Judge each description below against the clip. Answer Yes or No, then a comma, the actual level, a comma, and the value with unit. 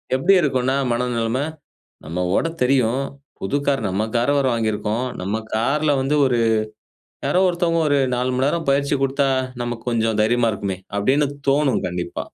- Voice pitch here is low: Yes, low, 125 Hz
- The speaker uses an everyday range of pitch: Yes, average, 4.0 semitones